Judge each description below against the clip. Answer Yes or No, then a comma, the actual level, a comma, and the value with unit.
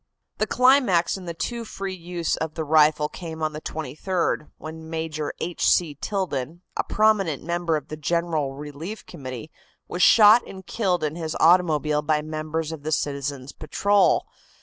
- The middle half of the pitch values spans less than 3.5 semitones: Yes, average, 3.0 semitones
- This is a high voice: No, medium, 160 Hz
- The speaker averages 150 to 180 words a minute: Yes, average, 165 wpm